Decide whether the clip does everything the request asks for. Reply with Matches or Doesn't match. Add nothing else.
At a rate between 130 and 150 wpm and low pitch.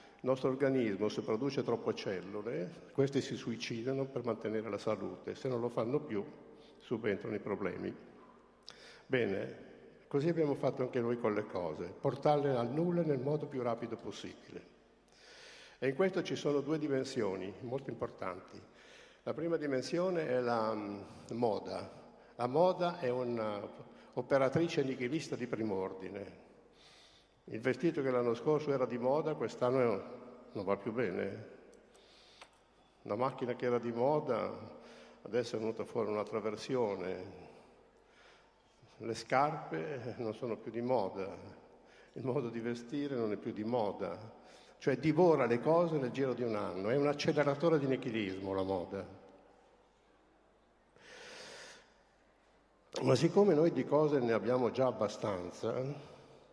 Matches